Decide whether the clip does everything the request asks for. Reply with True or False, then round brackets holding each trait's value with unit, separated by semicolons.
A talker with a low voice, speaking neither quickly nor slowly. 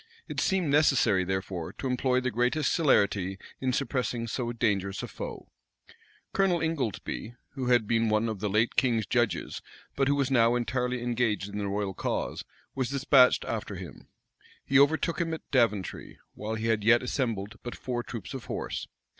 True (120 Hz; 170 wpm)